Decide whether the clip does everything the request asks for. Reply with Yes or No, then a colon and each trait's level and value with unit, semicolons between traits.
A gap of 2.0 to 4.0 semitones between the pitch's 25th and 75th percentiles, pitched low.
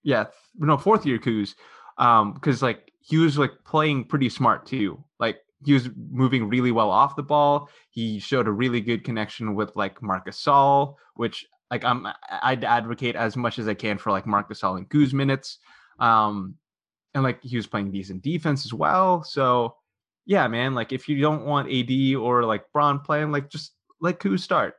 No: average, 4.6 semitones; low, 130 Hz